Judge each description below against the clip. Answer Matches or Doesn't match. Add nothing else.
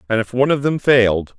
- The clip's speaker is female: Doesn't match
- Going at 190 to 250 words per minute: Doesn't match